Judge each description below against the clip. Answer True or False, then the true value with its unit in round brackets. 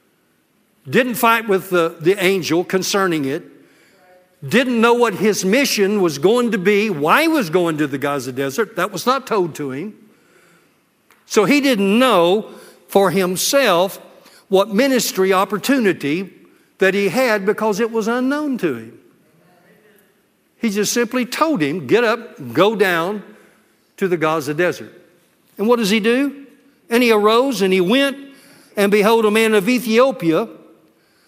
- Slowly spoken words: False (150 wpm)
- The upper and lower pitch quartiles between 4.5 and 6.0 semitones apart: True (4.8 semitones)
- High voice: True (210 Hz)